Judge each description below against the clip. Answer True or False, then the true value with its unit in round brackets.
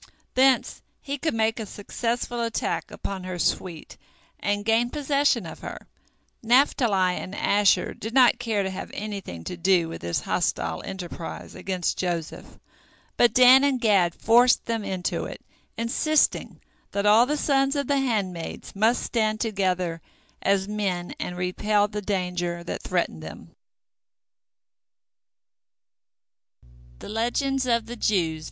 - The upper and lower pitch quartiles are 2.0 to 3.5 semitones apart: False (4.8 semitones)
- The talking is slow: True (125 wpm)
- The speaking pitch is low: False (205 Hz)